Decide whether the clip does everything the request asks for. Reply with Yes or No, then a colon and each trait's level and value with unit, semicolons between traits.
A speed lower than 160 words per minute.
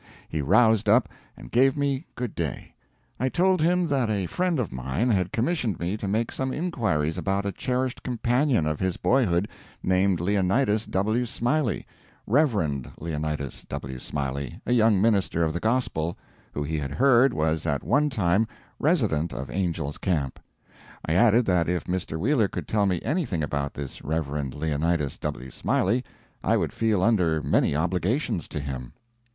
No: average, 165 wpm